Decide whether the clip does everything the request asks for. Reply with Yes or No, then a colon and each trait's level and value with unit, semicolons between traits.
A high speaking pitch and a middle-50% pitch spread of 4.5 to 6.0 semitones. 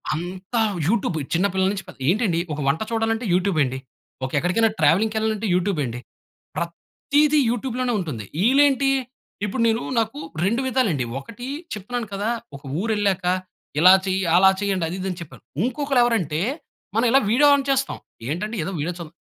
Yes: high, 205 Hz; average, 5.0 semitones